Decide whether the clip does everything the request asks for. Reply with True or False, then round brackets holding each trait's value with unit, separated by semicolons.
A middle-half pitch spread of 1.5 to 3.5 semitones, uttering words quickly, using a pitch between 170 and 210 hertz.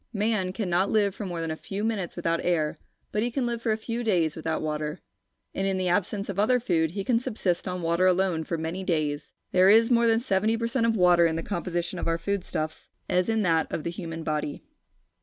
False (4.5 semitones; 230 wpm; 185 Hz)